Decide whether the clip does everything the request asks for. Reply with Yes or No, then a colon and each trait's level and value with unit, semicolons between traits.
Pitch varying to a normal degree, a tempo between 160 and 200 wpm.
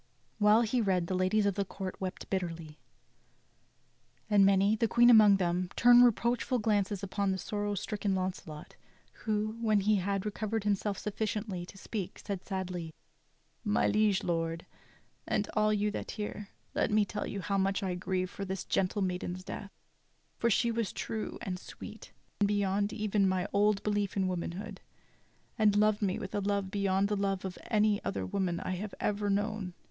No: narrow, 2.1 semitones; average, 175 wpm